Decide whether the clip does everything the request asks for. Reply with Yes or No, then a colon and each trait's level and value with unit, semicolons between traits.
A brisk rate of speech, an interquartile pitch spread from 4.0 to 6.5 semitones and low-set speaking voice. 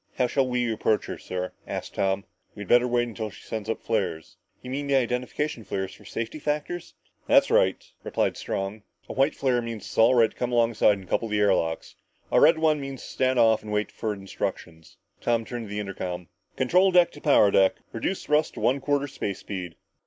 Yes: fast, 210 wpm; average, 4.7 semitones; low, 115 Hz